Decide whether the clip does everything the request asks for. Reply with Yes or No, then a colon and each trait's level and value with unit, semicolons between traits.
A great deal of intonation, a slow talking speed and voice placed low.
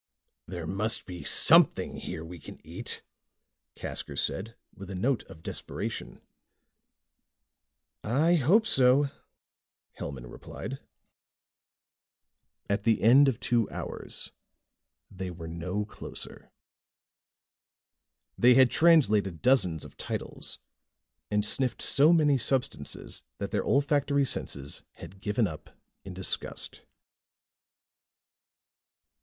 Yes: wide, 6.7 semitones; slow, 105 wpm; low, 110 Hz